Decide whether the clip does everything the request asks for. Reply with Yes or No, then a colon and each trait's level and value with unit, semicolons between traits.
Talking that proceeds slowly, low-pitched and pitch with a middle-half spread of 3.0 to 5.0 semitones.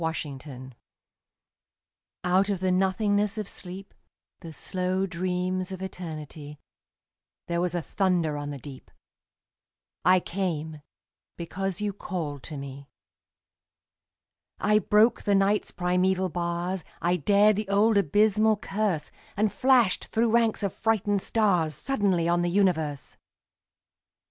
No: slow, 125 wpm; medium, 185 Hz; average, 3.3 semitones